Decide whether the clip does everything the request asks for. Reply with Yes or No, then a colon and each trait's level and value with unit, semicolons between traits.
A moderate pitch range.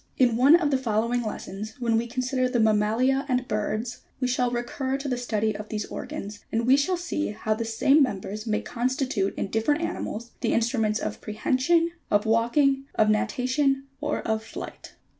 Yes: average, 3.6 semitones